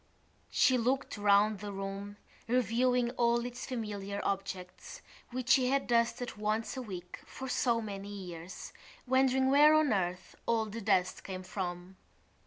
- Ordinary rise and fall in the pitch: Yes, average, 4.1 semitones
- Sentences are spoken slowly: No, average, 145 wpm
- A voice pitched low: No, high, 215 Hz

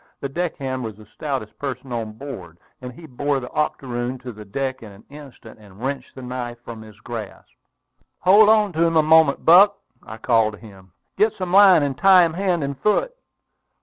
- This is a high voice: No, low, 135 Hz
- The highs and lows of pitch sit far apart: Yes, wide, 6.5 semitones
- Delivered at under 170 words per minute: No, average, 200 wpm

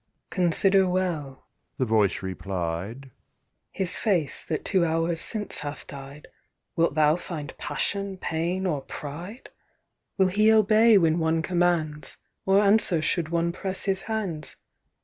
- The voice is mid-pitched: Yes, medium, 170 Hz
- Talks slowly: Yes, slow, 130 wpm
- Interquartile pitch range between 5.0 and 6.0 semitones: No, average, 4.3 semitones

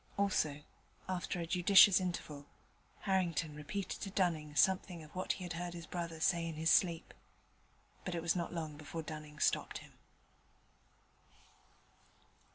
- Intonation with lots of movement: No, average, 2.8 semitones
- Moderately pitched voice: Yes, medium, 170 Hz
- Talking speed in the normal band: Yes, average, 145 wpm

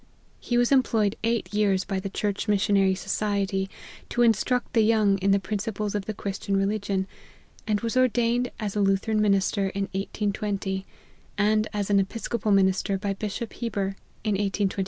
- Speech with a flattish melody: Yes, narrow, 1.7 semitones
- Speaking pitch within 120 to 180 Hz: No, high, 205 Hz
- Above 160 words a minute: Yes, average, 170 wpm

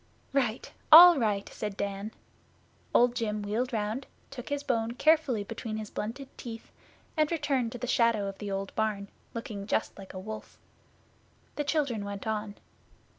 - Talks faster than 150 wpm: Yes, average, 160 wpm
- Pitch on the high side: Yes, high, 225 Hz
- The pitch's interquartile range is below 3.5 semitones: No, average, 3.8 semitones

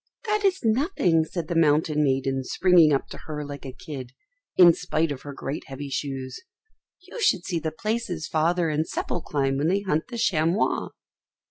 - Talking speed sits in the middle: Yes, average, 180 wpm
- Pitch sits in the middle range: Yes, medium, 160 Hz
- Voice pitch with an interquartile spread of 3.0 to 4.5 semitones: Yes, average, 4.2 semitones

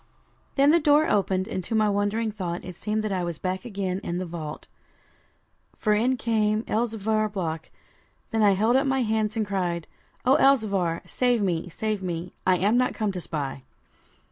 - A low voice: No, high, 205 Hz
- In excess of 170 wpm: Yes, average, 185 wpm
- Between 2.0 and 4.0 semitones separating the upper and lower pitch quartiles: Yes, average, 3.5 semitones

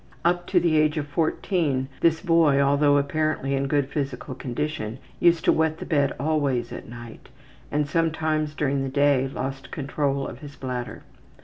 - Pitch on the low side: No, medium, 145 Hz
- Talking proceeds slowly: No, average, 170 wpm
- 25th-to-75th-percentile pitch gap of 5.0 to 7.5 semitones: No, narrow, 2.6 semitones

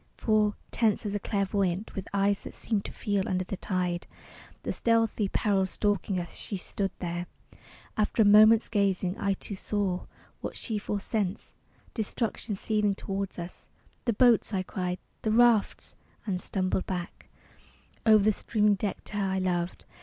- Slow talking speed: No, average, 160 wpm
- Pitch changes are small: Yes, narrow, 2.3 semitones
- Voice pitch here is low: No, high, 200 Hz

